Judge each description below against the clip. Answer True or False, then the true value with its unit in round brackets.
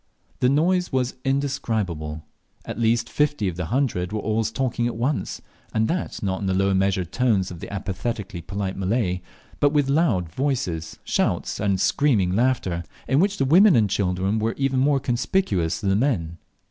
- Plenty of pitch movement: True (6.2 semitones)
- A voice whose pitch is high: False (110 Hz)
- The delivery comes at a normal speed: True (175 wpm)